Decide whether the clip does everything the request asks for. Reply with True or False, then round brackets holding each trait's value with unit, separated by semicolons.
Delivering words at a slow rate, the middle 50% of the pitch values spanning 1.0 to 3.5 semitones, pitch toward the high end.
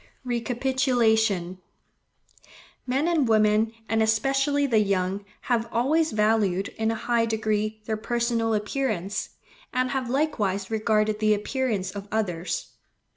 True (115 wpm; 2.9 semitones; 220 Hz)